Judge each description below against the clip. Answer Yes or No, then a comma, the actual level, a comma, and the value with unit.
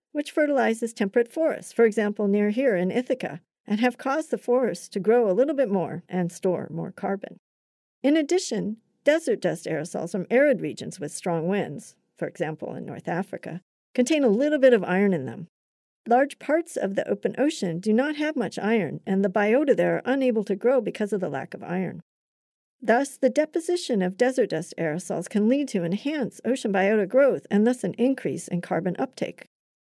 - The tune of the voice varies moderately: No, wide, 5.7 semitones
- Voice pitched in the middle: No, high, 225 Hz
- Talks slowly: No, average, 190 wpm